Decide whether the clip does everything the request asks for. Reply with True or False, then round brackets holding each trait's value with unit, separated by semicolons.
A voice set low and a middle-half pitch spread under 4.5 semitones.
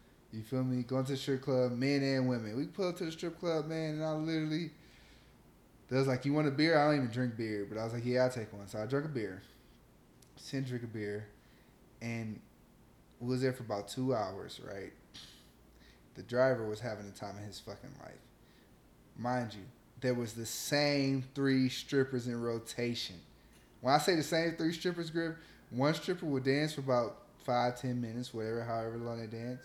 True (125 Hz; 3.7 semitones)